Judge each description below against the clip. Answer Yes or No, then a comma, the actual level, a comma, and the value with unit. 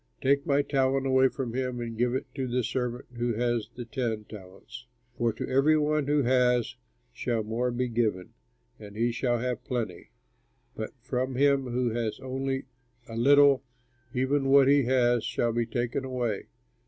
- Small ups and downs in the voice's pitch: Yes, narrow, 2.1 semitones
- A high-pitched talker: No, low, 125 Hz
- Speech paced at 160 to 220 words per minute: Yes, average, 170 wpm